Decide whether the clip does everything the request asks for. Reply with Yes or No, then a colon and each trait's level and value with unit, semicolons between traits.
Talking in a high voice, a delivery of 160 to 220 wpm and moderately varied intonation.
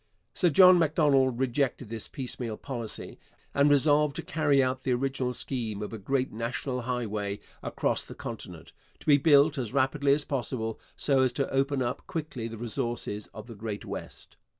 No: low, 130 Hz; average, 175 wpm; average, 3.3 semitones